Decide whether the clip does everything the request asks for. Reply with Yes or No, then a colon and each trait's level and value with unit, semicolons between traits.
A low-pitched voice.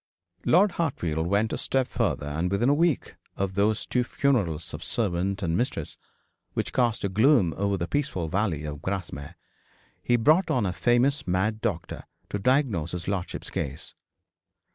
Yes: low, 100 Hz